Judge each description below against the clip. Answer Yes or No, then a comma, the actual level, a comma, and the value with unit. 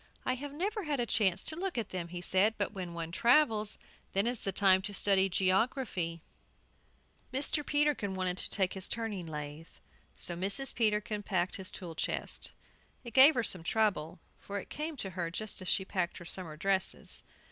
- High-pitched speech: Yes, high, 195 Hz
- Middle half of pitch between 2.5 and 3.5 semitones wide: No, average, 4.7 semitones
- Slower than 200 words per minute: Yes, average, 190 wpm